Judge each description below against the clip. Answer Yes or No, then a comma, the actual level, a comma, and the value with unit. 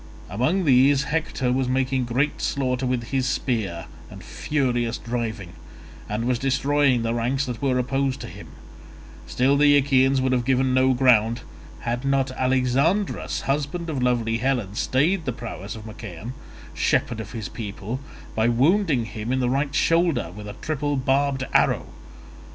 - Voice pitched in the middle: No, low, 130 Hz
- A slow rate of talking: No, average, 155 wpm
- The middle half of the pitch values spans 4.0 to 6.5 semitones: No, average, 2.8 semitones